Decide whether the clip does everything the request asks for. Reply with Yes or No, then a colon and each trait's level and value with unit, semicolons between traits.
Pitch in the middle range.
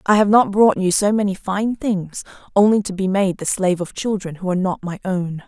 No: high, 195 Hz